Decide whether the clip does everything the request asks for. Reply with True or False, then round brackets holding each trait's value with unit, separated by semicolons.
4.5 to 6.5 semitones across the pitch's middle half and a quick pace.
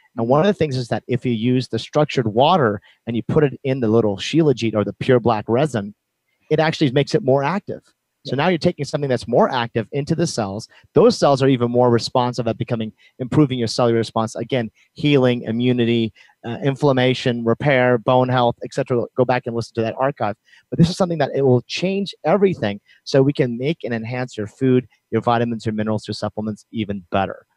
False (3.5 semitones; 210 wpm)